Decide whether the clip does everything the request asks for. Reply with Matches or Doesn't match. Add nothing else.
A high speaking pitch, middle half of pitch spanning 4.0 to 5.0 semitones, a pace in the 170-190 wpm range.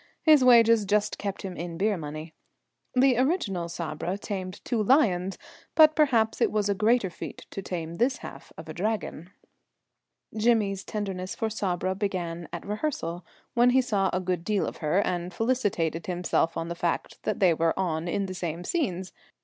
Matches